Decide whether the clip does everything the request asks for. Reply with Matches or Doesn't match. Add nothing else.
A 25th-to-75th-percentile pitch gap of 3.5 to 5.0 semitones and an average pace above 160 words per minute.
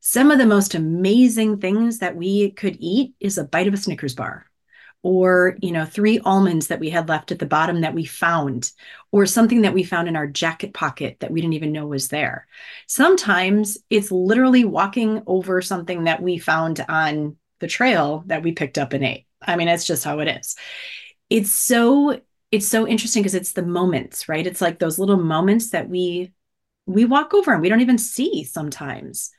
Matches